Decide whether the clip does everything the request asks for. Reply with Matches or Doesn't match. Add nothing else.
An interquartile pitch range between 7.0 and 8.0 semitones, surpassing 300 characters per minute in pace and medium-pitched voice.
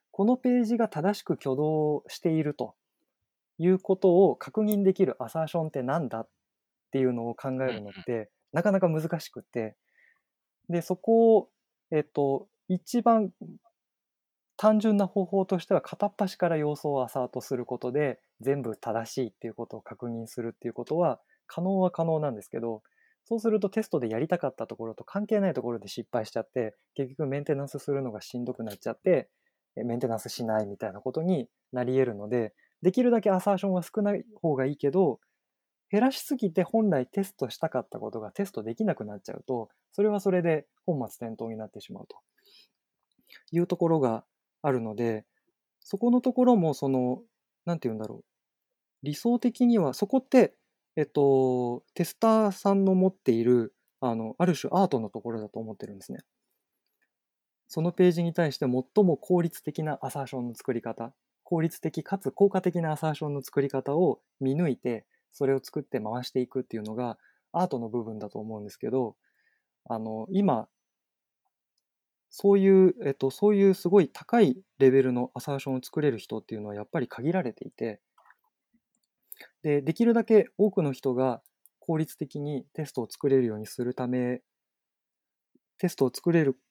Matches